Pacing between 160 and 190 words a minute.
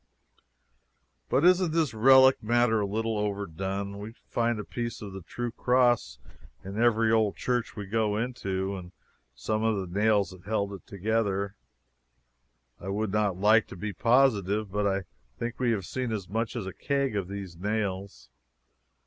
Yes: average, 165 wpm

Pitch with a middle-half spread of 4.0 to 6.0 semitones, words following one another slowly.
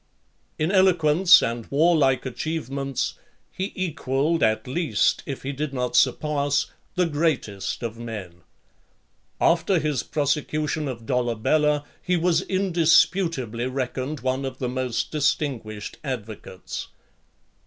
Yes: average, 4.3 semitones; slow, 115 wpm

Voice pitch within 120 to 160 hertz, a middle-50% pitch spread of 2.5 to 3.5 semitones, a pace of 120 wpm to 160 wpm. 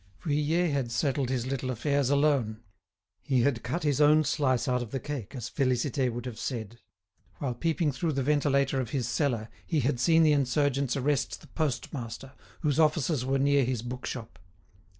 No: low, 135 Hz; average, 3.0 semitones; average, 175 wpm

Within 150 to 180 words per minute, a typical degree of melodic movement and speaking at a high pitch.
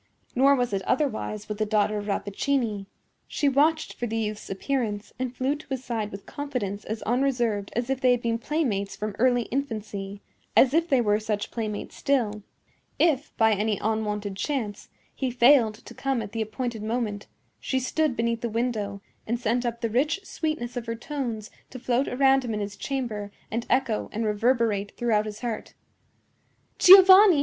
Yes: average, 175 wpm; average, 3.8 semitones; high, 235 Hz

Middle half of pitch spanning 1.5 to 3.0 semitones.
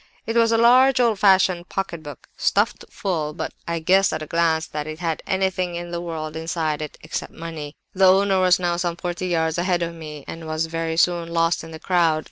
Yes: narrow, 2.5 semitones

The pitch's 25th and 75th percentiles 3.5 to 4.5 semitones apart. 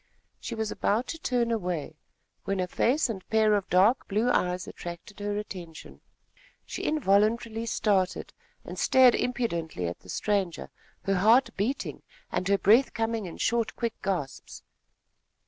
Yes: average, 4.1 semitones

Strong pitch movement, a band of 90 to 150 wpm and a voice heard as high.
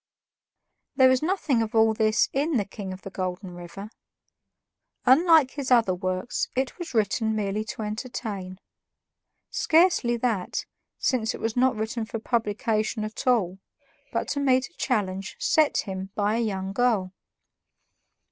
No: average, 4.5 semitones; average, 145 wpm; high, 220 Hz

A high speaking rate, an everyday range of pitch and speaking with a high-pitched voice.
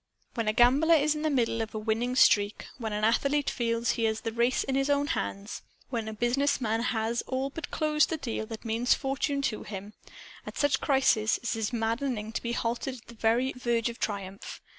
Yes: fast, 215 wpm; average, 3.5 semitones; high, 235 Hz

